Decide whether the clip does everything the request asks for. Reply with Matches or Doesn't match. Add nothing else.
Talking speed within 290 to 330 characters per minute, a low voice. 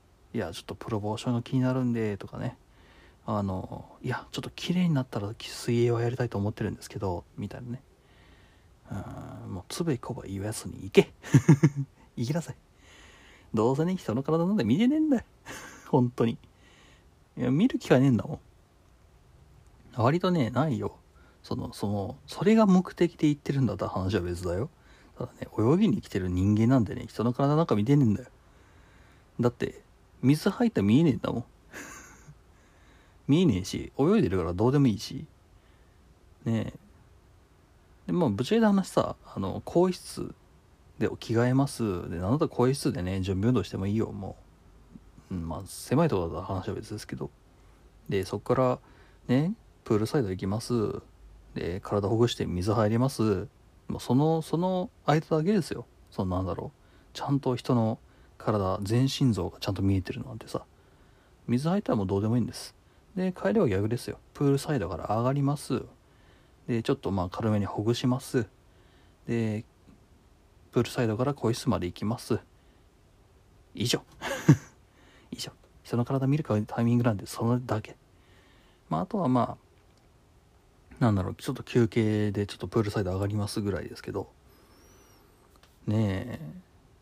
Matches